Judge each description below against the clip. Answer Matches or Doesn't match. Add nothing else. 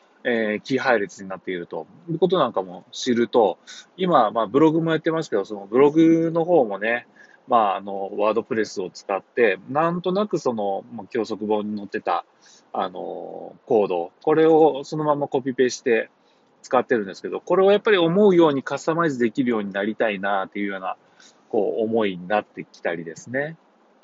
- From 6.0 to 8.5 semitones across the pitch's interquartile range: Matches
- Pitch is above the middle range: Doesn't match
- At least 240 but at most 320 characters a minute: Doesn't match